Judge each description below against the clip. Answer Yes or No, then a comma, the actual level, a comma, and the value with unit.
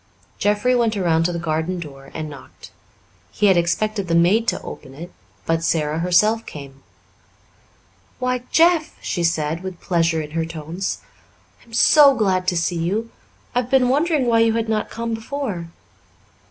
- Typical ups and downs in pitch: No, wide, 5.7 semitones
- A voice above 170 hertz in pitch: Yes, medium, 185 Hz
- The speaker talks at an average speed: Yes, average, 170 wpm